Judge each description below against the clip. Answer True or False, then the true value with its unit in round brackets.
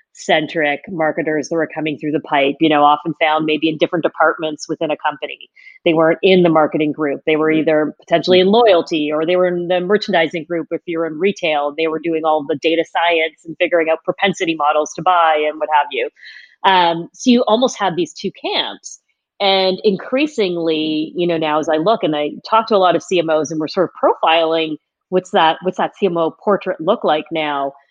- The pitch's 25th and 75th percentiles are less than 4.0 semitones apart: True (2.8 semitones)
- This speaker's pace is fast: True (210 wpm)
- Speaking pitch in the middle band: True (165 Hz)